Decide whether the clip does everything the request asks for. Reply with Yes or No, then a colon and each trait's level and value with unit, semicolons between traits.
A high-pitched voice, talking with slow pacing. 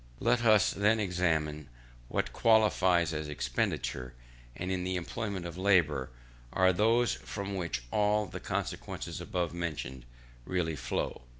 No: very low, 90 Hz; slow, 130 wpm